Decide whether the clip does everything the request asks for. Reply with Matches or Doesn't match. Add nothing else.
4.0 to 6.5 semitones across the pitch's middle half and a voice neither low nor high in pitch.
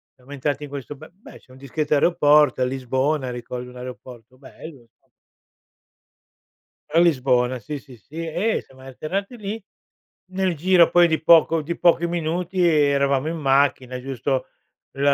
Matches